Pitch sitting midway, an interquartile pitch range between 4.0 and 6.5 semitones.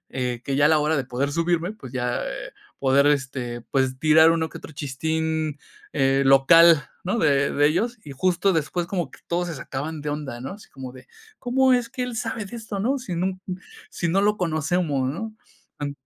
Yes: medium, 160 Hz; average, 5.0 semitones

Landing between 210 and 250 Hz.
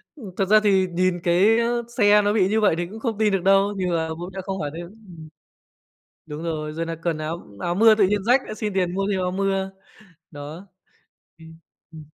No: high, 190 Hz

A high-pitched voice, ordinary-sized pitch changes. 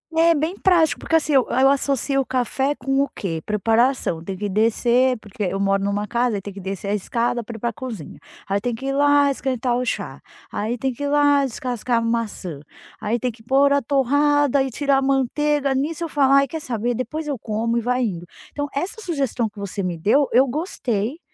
Yes: very high, 250 Hz; average, 4.5 semitones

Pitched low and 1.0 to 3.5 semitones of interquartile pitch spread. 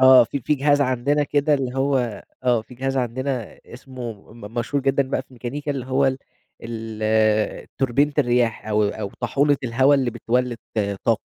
Yes: low, 130 Hz; average, 2.8 semitones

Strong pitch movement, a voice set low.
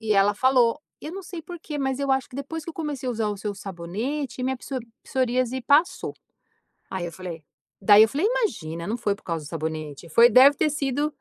No: wide, 6.3 semitones; very high, 250 Hz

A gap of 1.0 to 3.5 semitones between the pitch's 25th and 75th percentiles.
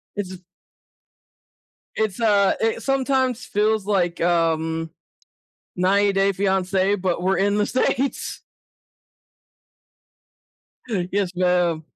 Yes: average, 2.7 semitones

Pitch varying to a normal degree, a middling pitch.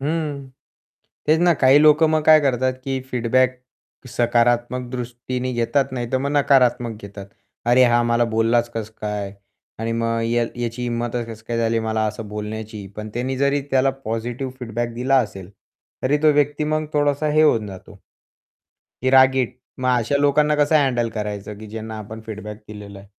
No: average, 3.3 semitones; low, 120 Hz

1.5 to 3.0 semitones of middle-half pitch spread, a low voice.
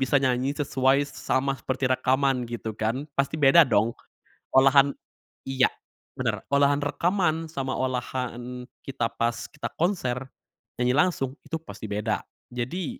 Yes: narrow, 2.4 semitones; low, 130 Hz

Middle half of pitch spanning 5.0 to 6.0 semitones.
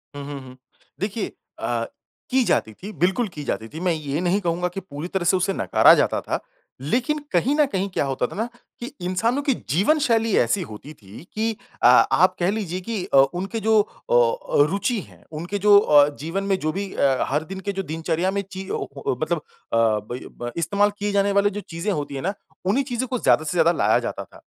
Yes: wide, 5.5 semitones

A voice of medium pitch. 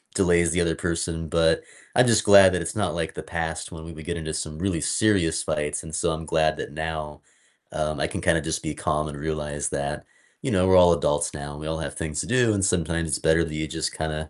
No: very low, 80 Hz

